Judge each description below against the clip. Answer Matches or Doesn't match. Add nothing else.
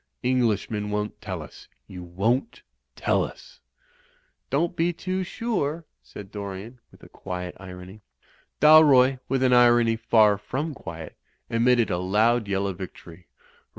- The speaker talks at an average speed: Matches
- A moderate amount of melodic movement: Doesn't match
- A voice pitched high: Doesn't match